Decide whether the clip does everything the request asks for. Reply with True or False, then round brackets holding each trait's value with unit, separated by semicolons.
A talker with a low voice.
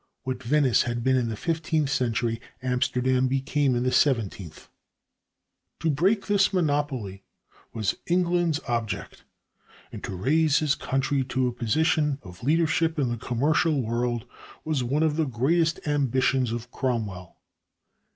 True (130 Hz)